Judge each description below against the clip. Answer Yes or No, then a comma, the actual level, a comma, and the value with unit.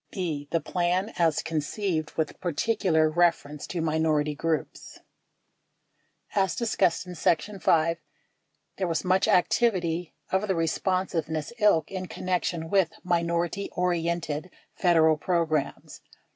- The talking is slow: Yes, slow, 120 wpm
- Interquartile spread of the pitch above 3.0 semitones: No, narrow, 2.5 semitones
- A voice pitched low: No, medium, 170 Hz